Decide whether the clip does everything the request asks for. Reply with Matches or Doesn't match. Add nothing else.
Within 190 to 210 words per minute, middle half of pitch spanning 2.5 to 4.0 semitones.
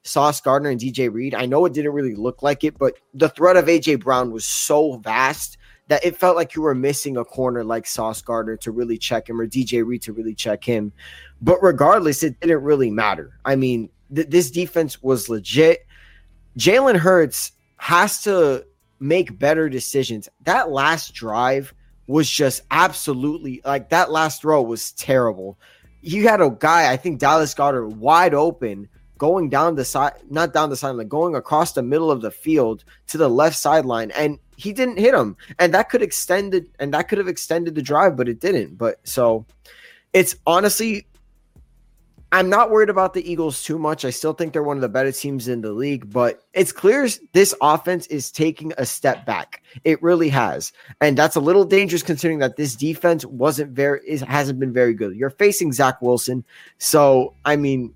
Doesn't match